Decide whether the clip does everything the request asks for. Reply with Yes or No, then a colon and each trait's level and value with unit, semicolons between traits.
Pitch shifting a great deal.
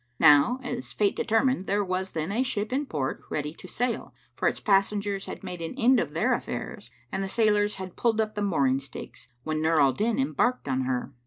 Yes: wide, 6.3 semitones